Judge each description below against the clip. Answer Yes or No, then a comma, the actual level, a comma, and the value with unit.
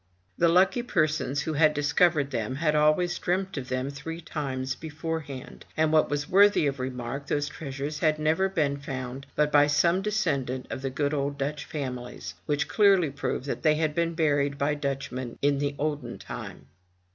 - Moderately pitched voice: Yes, medium, 145 Hz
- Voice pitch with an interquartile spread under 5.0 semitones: Yes, average, 2.7 semitones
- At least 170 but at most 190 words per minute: Yes, average, 180 wpm